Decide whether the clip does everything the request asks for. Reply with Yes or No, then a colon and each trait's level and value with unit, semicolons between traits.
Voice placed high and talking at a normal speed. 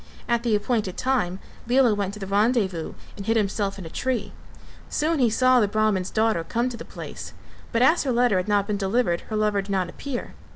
No: high, 215 Hz; fast, 220 wpm